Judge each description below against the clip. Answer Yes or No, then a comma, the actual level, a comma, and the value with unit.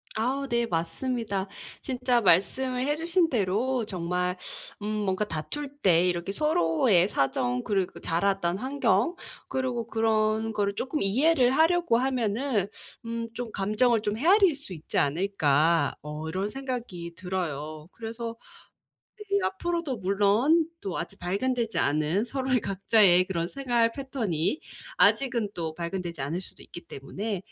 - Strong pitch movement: Yes, wide, 6.3 semitones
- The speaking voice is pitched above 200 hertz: Yes, high, 210 Hz